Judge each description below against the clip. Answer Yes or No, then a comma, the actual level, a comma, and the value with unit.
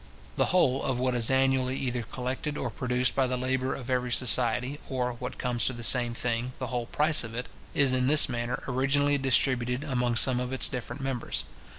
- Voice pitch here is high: No, low, 125 Hz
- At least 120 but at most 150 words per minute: No, fast, 205 wpm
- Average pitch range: No, narrow, 1.4 semitones